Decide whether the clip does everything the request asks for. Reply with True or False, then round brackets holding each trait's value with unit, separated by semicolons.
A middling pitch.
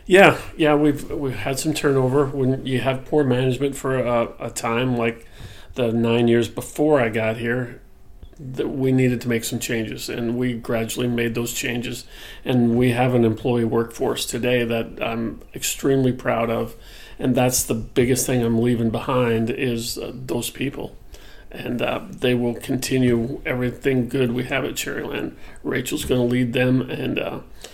False (125 Hz)